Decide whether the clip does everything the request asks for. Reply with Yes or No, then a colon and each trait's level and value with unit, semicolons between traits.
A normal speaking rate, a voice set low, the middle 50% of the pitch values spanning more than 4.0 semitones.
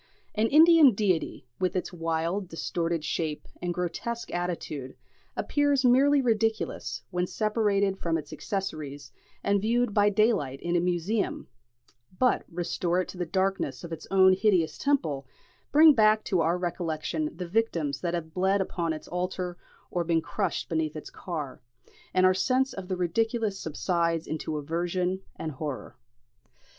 No: average, 150 wpm; medium, 180 Hz; average, 4.4 semitones